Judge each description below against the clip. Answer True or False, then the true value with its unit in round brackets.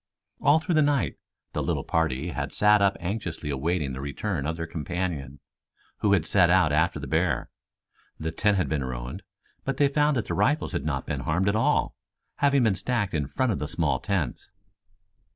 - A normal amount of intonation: False (6.0 semitones)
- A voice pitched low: True (90 Hz)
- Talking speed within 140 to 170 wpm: False (195 wpm)